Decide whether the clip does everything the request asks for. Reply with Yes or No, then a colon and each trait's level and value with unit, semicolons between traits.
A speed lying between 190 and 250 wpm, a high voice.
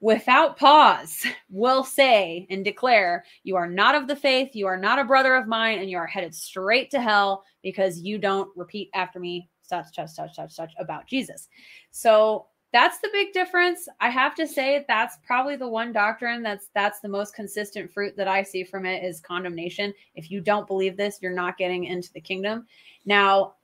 Yes: average, 200 wpm; high, 205 Hz